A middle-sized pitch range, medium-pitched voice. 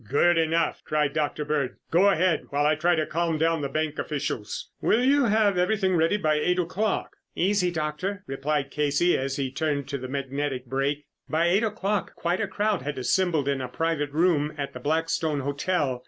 Yes: average, 4.0 semitones; medium, 155 Hz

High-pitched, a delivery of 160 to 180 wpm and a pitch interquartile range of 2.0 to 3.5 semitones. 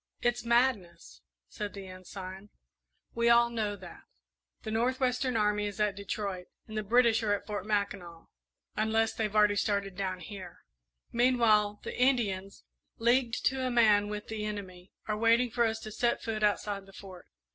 Yes: high, 210 Hz; average, 170 wpm; average, 2.9 semitones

